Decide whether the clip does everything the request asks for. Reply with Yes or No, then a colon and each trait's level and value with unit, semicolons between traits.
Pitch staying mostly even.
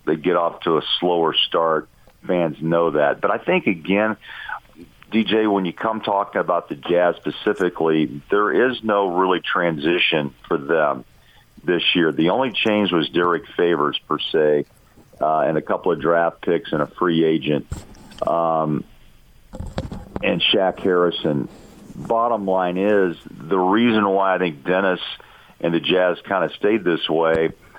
No: average, 3.4 semitones